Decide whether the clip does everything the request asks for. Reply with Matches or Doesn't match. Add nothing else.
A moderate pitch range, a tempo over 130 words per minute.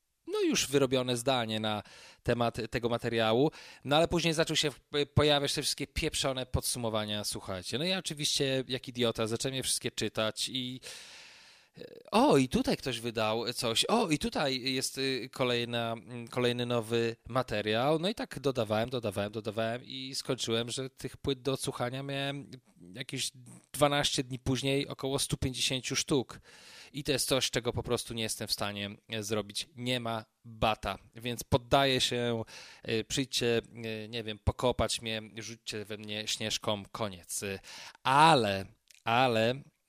Matches